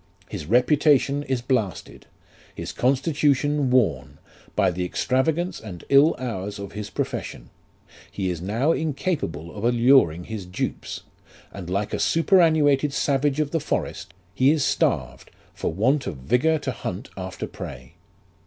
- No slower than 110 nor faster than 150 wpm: Yes, average, 140 wpm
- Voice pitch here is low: Yes, low, 130 Hz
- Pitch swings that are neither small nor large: No, wide, 6.9 semitones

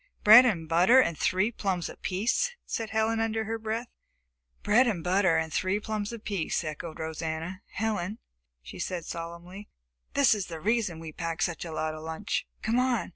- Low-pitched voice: No, high, 190 Hz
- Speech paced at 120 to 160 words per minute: No, average, 175 wpm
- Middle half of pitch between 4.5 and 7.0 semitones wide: Yes, average, 5.0 semitones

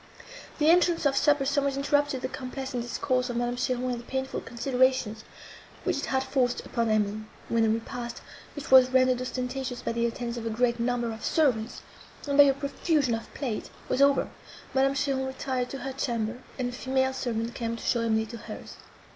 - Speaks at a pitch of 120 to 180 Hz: No, very high, 255 Hz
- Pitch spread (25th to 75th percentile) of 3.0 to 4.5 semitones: No, narrow, 2.5 semitones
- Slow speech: No, average, 195 wpm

